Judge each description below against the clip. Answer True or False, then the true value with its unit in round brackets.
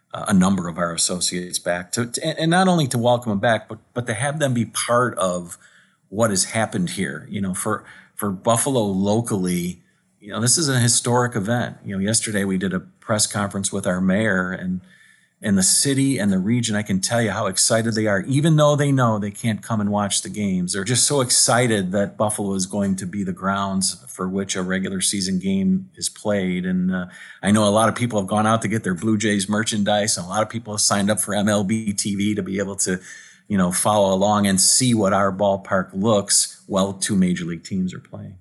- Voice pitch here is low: True (105 Hz)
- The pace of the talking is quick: True (225 wpm)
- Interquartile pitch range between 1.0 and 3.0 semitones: False (3.8 semitones)